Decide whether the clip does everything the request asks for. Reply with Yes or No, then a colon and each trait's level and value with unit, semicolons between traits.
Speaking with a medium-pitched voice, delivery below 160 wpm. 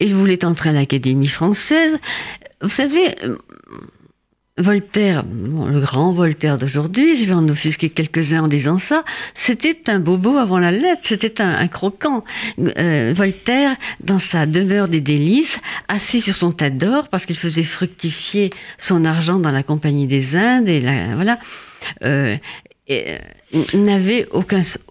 Yes: medium, 180 Hz; average, 150 wpm